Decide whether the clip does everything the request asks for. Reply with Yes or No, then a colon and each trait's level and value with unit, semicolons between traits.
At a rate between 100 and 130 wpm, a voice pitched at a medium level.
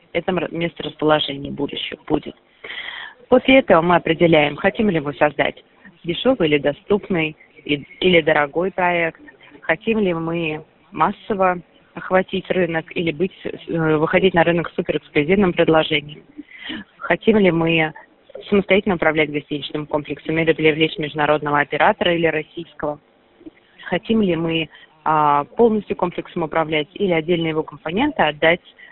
Yes: average, 120 wpm; medium, 165 Hz